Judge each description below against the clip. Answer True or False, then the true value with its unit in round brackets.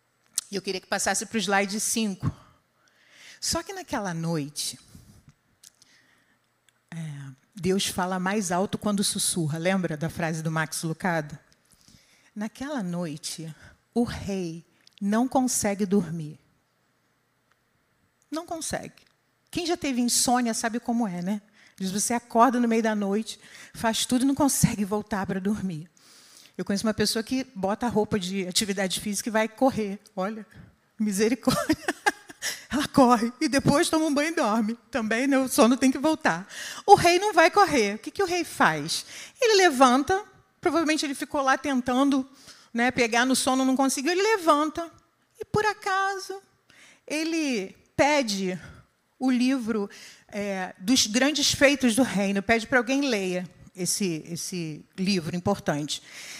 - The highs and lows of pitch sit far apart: True (6.5 semitones)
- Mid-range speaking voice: False (220 Hz)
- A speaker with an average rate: True (145 wpm)